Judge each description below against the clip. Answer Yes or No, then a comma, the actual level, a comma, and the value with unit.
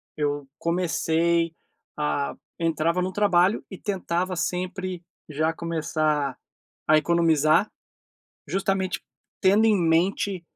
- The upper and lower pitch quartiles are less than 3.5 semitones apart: Yes, average, 2.9 semitones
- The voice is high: No, medium, 170 Hz